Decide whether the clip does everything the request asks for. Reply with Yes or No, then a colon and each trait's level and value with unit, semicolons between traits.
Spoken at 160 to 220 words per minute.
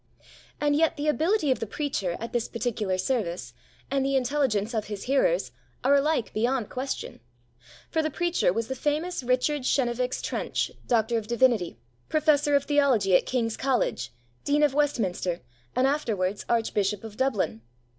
No: average, 150 wpm